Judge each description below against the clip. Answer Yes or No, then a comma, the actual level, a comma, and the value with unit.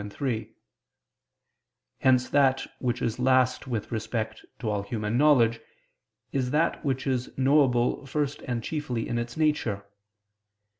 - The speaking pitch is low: Yes, low, 125 Hz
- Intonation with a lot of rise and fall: No, average, 3.0 semitones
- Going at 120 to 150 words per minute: Yes, slow, 135 wpm